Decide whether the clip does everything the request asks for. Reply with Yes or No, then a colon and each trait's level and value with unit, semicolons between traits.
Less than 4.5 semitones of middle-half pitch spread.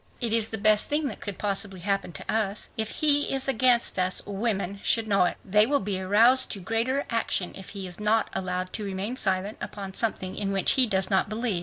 Yes: average, 3.1 semitones